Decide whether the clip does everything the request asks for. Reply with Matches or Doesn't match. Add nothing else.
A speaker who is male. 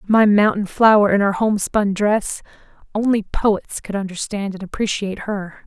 Doesn't match